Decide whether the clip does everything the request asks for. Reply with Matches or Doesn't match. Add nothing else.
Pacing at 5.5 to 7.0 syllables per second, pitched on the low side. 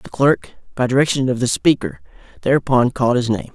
Matches